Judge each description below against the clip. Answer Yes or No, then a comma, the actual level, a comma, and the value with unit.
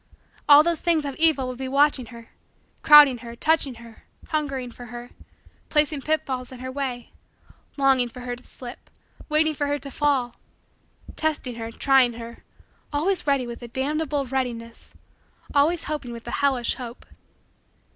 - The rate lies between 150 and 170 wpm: Yes, average, 155 wpm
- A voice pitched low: No, very high, 265 Hz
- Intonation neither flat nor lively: Yes, average, 3.4 semitones